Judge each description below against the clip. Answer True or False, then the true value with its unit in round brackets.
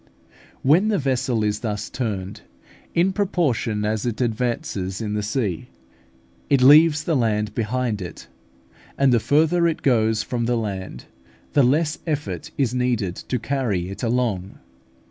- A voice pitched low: True (120 Hz)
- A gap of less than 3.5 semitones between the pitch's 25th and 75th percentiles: False (5.0 semitones)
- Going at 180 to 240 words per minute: False (145 wpm)